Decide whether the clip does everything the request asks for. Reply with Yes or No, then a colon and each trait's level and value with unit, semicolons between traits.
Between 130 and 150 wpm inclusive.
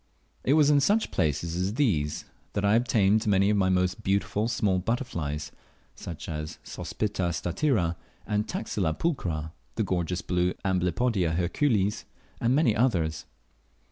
Yes: average, 140 wpm